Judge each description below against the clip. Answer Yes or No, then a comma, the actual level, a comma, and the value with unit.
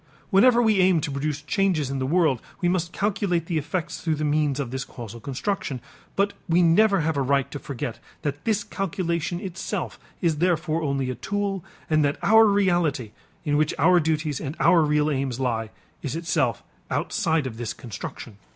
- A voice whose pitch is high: No, medium, 155 Hz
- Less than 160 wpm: No, average, 185 wpm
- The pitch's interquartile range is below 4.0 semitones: No, average, 4.7 semitones